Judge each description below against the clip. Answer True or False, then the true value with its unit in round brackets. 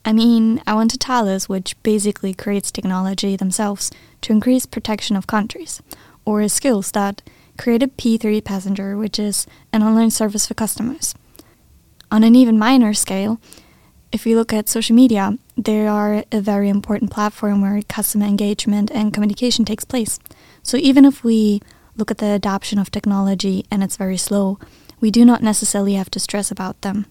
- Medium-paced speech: True (175 wpm)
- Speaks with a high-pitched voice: True (210 Hz)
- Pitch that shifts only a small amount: True (2.0 semitones)